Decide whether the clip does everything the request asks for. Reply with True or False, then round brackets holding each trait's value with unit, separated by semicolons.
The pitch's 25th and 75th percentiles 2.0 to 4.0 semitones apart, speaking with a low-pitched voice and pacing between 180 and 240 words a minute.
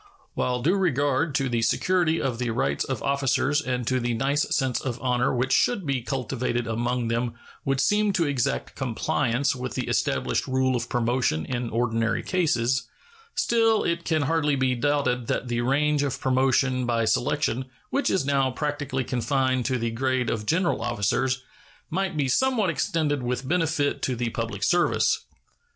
False (3.3 semitones; 130 Hz; 170 wpm)